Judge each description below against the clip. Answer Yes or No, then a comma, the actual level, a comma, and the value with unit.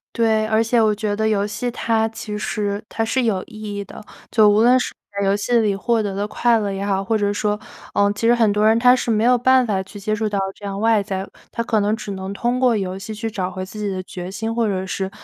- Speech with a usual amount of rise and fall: No, narrow, 2.1 semitones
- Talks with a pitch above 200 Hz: Yes, high, 210 Hz